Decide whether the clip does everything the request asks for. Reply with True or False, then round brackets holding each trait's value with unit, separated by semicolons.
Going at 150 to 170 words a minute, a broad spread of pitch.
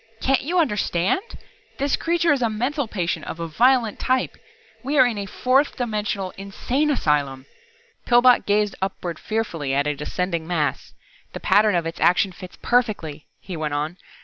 True (165 wpm; 7.0 semitones)